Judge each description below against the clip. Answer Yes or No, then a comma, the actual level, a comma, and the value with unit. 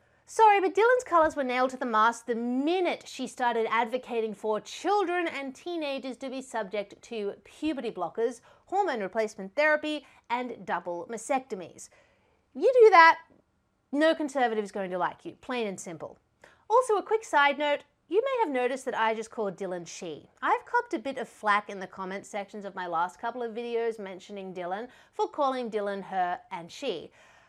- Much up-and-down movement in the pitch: Yes, wide, 6.6 semitones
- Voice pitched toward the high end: Yes, high, 240 Hz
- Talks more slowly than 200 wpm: Yes, average, 180 wpm